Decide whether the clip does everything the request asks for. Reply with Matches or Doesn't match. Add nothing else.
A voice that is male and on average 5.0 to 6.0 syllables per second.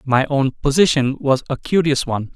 Matches